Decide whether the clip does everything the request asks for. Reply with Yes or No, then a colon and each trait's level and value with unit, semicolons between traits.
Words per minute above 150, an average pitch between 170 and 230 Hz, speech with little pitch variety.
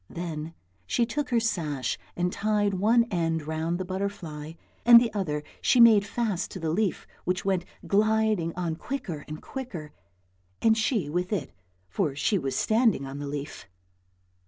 No: average, 160 wpm; medium, 185 Hz; wide, 5.5 semitones